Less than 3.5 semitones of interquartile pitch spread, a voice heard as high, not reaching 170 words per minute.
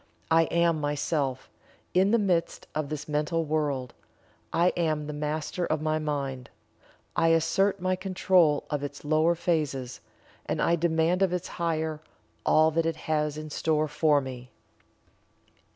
No: narrow, 2.4 semitones; medium, 155 Hz; average, 150 wpm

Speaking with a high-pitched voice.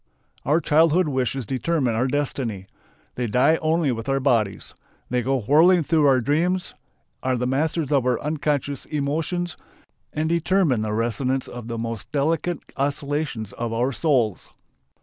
No: medium, 140 Hz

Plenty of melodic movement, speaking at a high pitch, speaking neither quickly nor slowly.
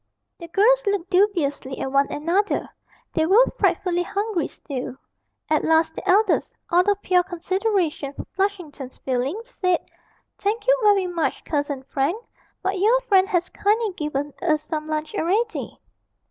No: average, 5.0 semitones; very high, 360 Hz; average, 145 wpm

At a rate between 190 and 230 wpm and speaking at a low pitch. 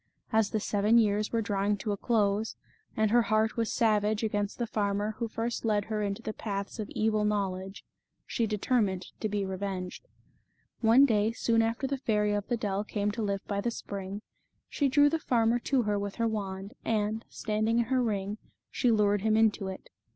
No: average, 195 wpm; high, 215 Hz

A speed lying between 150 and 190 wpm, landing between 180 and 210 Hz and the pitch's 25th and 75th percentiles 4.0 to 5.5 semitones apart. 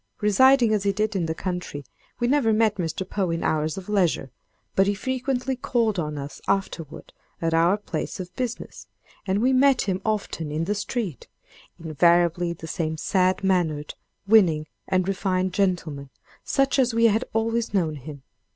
Yes: average, 165 wpm; high, 190 Hz; average, 5.1 semitones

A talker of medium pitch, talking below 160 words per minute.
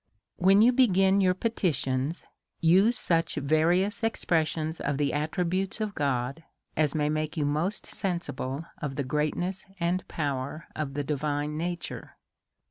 Yes: medium, 160 Hz; average, 140 wpm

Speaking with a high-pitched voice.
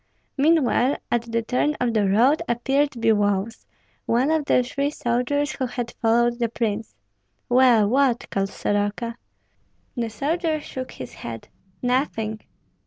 Yes: high, 240 Hz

